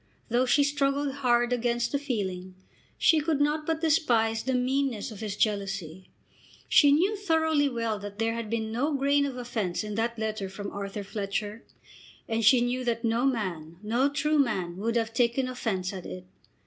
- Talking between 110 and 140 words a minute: No, average, 180 wpm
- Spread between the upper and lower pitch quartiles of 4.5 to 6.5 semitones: Yes, average, 4.9 semitones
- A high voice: Yes, high, 235 Hz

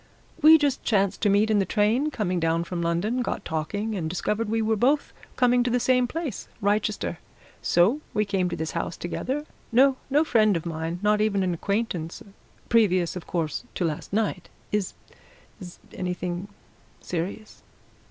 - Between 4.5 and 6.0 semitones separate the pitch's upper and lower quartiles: Yes, average, 4.8 semitones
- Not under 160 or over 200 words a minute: Yes, average, 170 wpm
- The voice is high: Yes, high, 205 Hz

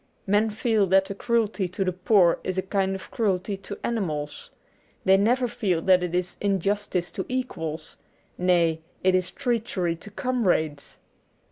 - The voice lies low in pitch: No, high, 190 Hz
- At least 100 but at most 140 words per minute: No, average, 155 wpm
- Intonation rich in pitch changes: No, average, 3.1 semitones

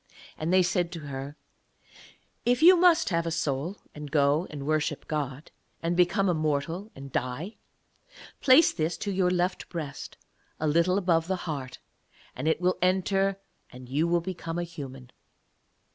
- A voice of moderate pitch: Yes, medium, 165 Hz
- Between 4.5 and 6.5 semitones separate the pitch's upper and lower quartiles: No, average, 4.0 semitones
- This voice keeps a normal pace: Yes, average, 160 wpm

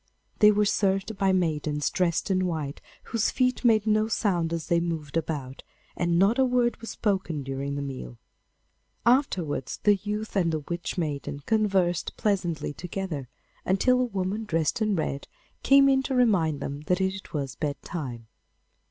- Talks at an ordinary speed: Yes, average, 160 wpm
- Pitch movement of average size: No, wide, 5.7 semitones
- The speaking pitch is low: No, medium, 185 Hz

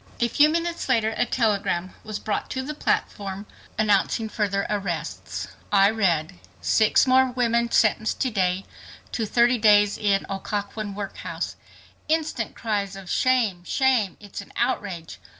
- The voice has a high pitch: Yes, high, 210 Hz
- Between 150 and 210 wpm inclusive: No, average, 140 wpm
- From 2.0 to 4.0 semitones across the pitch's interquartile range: Yes, average, 3.3 semitones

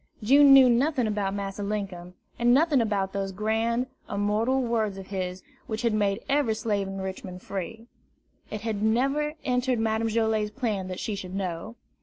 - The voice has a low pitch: No, high, 215 Hz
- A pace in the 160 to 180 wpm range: Yes, average, 170 wpm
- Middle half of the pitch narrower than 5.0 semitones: Yes, average, 3.3 semitones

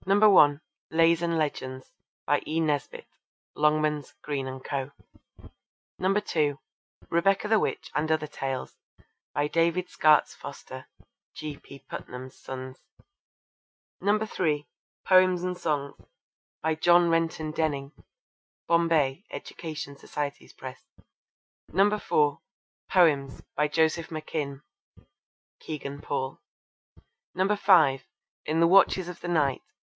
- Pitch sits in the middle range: Yes, medium, 155 Hz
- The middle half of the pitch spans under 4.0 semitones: Yes, average, 3.4 semitones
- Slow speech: Yes, slow, 105 wpm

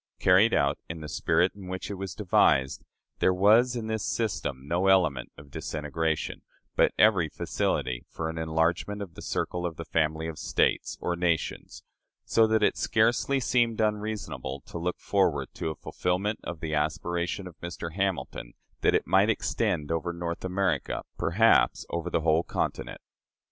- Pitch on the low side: Yes, very low, 85 Hz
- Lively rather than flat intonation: No, average, 3.9 semitones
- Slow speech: No, average, 165 wpm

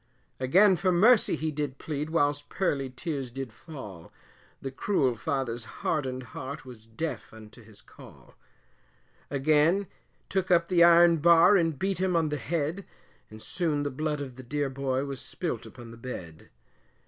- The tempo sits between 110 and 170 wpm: Yes, average, 160 wpm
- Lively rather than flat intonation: No, average, 4.6 semitones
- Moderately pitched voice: Yes, medium, 145 Hz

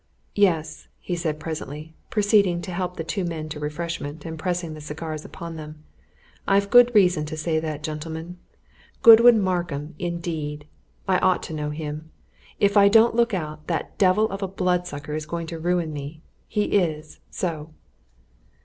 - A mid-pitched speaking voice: Yes, medium, 165 Hz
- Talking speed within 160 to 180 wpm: Yes, average, 165 wpm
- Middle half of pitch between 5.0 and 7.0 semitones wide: No, average, 3.1 semitones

